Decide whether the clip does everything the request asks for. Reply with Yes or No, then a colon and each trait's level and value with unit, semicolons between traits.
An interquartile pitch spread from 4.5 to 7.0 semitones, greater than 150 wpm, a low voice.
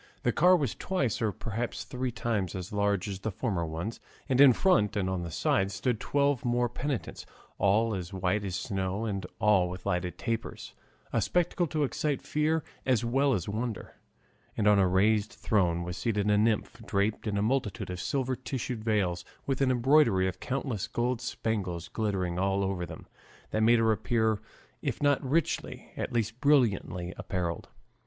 Yes: average, 4.8 semitones; average, 175 wpm; low, 110 Hz